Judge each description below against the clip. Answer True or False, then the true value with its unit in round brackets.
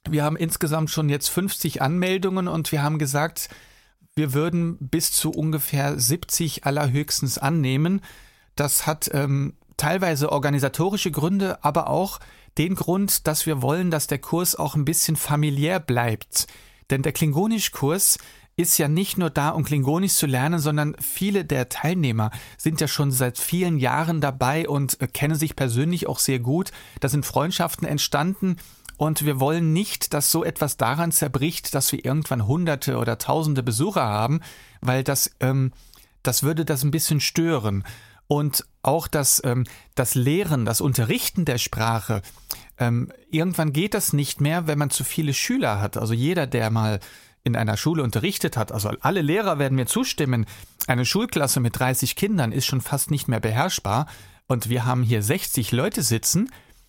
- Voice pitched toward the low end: False (145 Hz)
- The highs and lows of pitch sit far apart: False (4.1 semitones)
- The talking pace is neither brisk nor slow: True (165 wpm)